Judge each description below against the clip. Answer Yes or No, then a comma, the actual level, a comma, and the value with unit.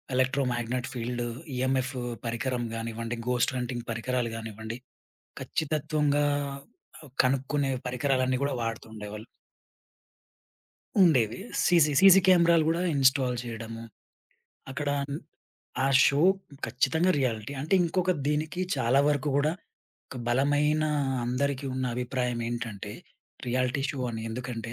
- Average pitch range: Yes, average, 3.5 semitones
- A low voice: Yes, low, 130 Hz